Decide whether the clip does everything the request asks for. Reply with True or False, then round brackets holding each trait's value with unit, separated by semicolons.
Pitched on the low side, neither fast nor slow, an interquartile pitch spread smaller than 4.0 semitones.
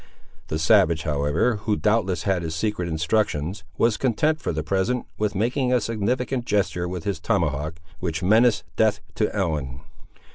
False (100 Hz; 155 wpm; 5.2 semitones)